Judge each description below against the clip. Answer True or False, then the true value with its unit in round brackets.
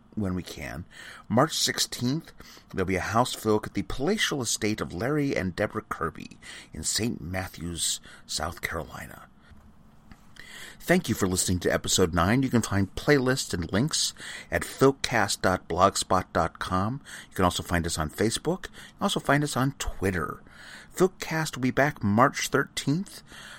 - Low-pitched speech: True (105 Hz)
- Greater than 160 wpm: False (150 wpm)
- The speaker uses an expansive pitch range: True (6.6 semitones)